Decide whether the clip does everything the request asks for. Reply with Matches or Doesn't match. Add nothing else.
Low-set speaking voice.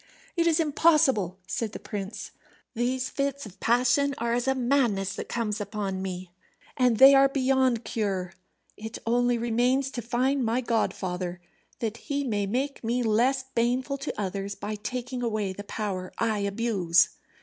Doesn't match